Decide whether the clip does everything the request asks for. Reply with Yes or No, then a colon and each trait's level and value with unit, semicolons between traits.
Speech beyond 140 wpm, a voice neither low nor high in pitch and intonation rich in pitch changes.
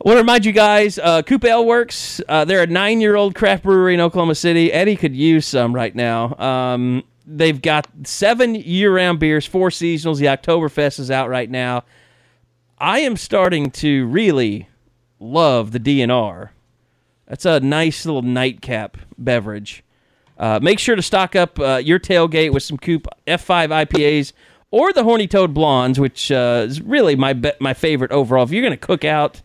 Yes: average, 175 wpm; medium, 155 Hz; wide, 6.1 semitones